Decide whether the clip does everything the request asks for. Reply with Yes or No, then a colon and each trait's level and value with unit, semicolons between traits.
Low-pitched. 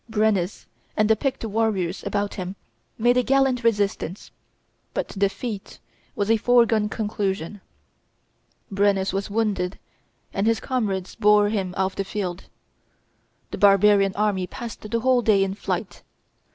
No: high, 205 Hz